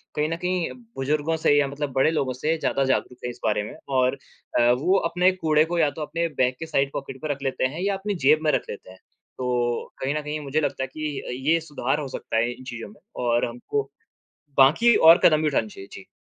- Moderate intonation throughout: Yes, average, 3.8 semitones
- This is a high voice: No, medium, 145 Hz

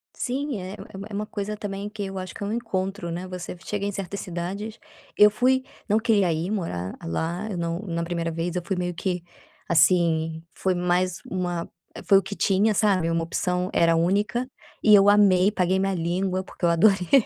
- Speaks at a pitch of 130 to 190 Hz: Yes, medium, 185 Hz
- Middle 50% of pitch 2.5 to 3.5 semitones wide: Yes, average, 2.9 semitones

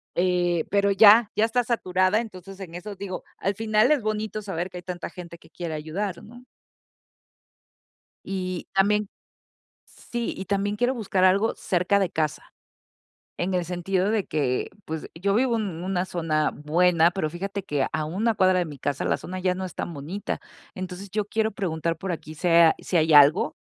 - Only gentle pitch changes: No, average, 3.2 semitones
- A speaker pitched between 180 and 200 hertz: Yes, medium, 185 Hz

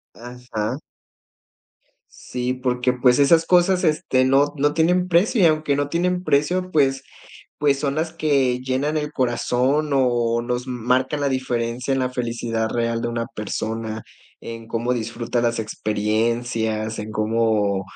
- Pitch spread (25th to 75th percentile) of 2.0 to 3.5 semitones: No, average, 3.9 semitones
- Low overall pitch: Yes, low, 125 Hz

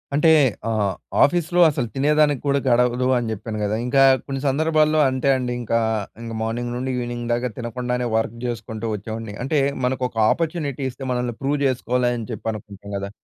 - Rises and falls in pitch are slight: No, average, 3.3 semitones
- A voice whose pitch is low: Yes, low, 125 Hz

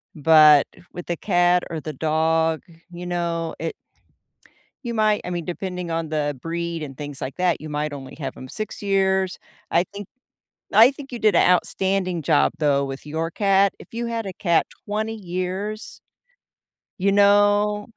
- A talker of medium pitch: Yes, medium, 175 Hz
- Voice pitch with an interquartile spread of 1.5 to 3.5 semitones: No, average, 4.1 semitones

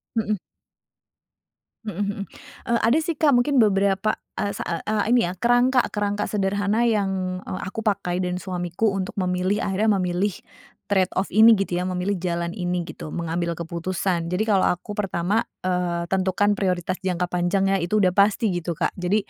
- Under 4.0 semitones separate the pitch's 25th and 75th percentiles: Yes, narrow, 2.6 semitones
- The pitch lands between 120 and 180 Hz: No, high, 190 Hz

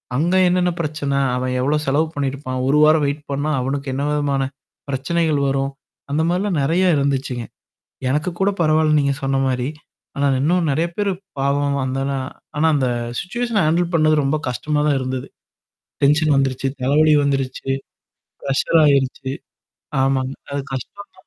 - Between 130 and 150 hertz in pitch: Yes, medium, 140 Hz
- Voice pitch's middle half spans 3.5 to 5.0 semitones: No, narrow, 2.5 semitones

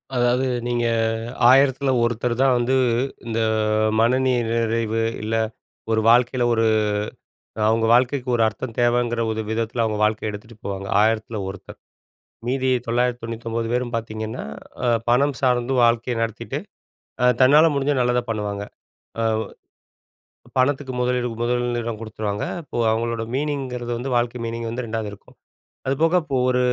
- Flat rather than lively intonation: Yes, narrow, 1.9 semitones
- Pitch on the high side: No, low, 120 Hz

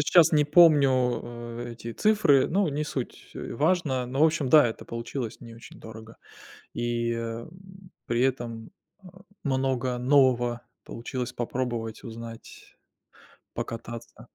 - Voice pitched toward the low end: Yes, low, 125 Hz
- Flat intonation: No, average, 4.2 semitones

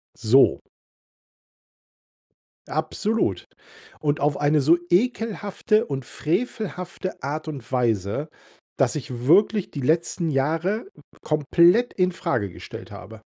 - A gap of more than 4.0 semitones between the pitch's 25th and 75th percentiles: Yes, wide, 5.5 semitones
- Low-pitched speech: No, medium, 155 Hz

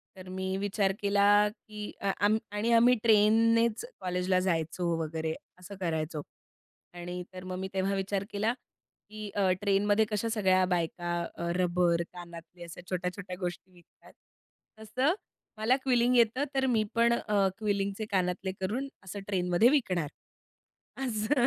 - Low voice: No, high, 195 Hz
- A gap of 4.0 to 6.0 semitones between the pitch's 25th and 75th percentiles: No, average, 3.3 semitones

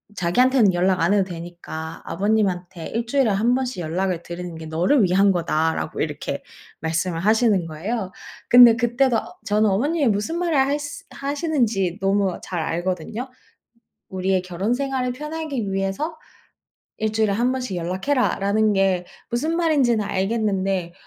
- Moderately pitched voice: No, high, 205 Hz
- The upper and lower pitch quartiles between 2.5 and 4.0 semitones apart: No, wide, 5.5 semitones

